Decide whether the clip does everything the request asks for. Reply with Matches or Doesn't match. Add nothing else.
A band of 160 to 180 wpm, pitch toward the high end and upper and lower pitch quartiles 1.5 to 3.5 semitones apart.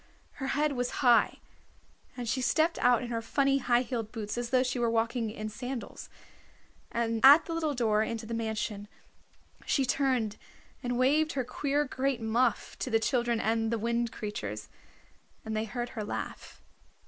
Matches